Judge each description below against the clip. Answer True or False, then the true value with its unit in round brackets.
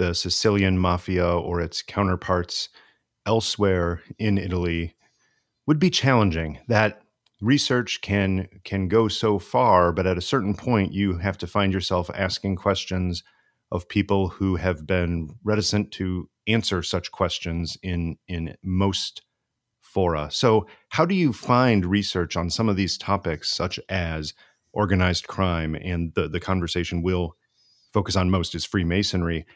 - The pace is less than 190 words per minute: True (140 wpm)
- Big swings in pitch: False (3.0 semitones)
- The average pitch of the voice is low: True (95 Hz)